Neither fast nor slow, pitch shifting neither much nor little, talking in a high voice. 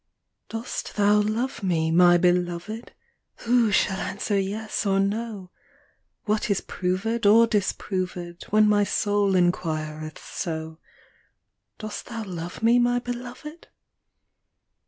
No: slow, 115 wpm; average, 4.0 semitones; high, 205 Hz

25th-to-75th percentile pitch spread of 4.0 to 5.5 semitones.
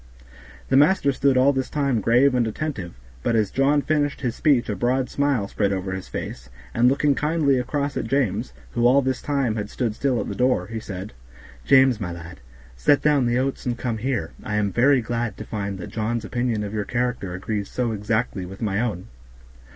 Yes: average, 4.5 semitones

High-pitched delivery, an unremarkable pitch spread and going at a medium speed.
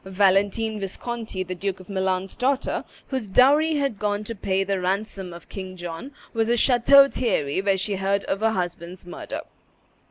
Yes: high, 200 Hz; average, 3.5 semitones; average, 170 wpm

